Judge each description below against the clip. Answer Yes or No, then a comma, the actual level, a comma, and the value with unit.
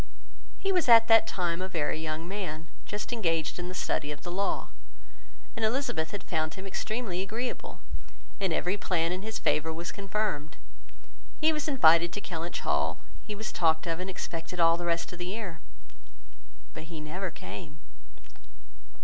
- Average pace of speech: Yes, average, 165 wpm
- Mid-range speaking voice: Yes, medium, 180 Hz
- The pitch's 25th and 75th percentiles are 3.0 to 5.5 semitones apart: Yes, average, 4.1 semitones